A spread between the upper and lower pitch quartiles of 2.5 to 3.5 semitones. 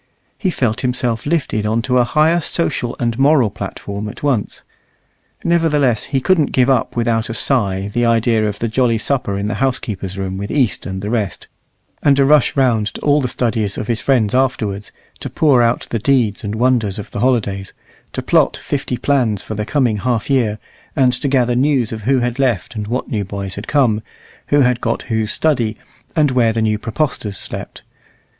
No: average, 3.9 semitones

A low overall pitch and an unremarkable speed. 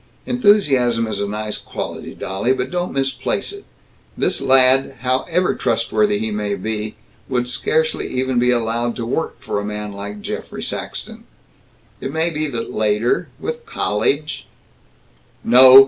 Yes: low, 125 Hz; average, 145 wpm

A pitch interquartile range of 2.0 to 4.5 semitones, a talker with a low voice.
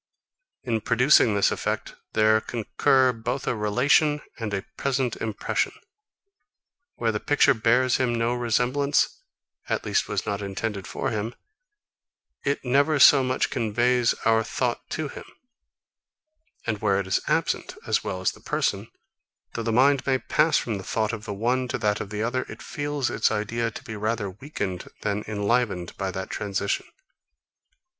Yes: average, 3.5 semitones; low, 115 Hz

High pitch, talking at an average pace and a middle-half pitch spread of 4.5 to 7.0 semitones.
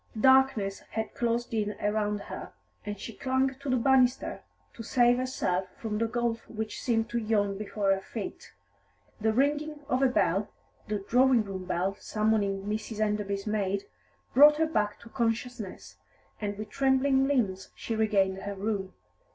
No: high, 220 Hz; average, 160 wpm; average, 3.8 semitones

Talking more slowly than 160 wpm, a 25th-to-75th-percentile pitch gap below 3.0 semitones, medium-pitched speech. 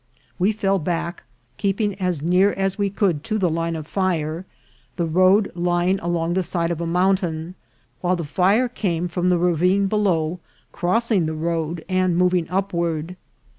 No: average, 165 wpm; narrow, 2.4 semitones; medium, 180 Hz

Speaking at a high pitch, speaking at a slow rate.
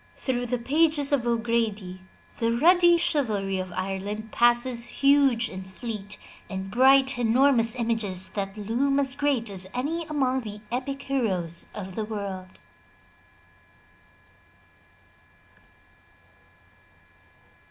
Yes: high, 235 Hz; slow, 105 wpm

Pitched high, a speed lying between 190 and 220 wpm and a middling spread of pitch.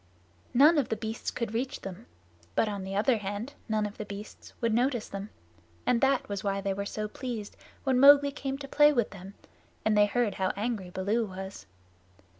Yes: high, 215 Hz; average, 200 wpm; average, 3.9 semitones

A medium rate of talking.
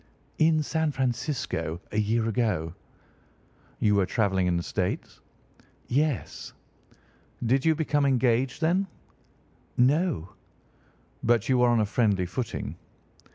No: slow, 115 wpm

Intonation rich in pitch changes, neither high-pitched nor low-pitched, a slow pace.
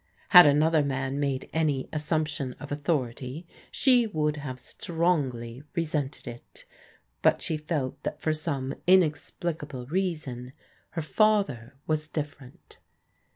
No: average, 3.5 semitones; medium, 150 Hz; slow, 120 wpm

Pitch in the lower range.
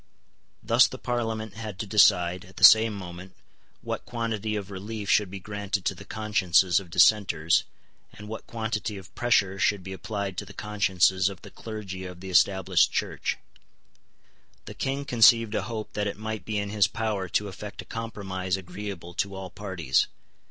Yes: low, 100 Hz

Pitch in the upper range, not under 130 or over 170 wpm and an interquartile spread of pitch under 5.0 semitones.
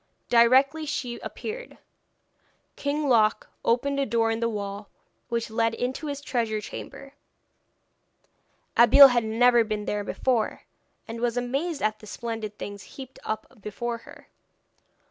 Yes: high, 235 Hz; slow, 135 wpm; average, 3.5 semitones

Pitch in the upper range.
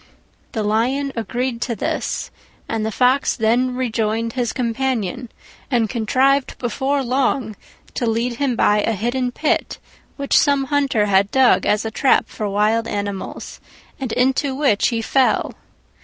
Yes: high, 240 Hz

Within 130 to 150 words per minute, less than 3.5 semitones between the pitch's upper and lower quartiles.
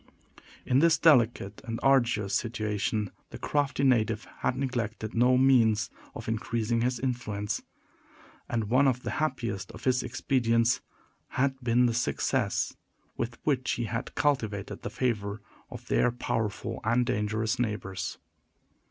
Yes: slow, 135 wpm; average, 2.8 semitones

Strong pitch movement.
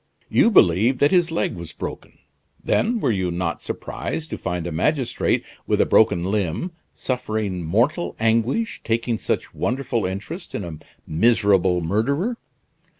Yes: wide, 7.5 semitones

